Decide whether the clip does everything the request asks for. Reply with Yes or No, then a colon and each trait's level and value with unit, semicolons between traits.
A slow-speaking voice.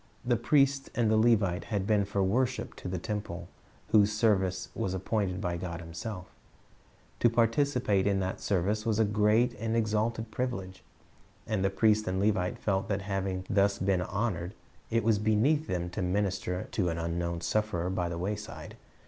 No: average, 175 wpm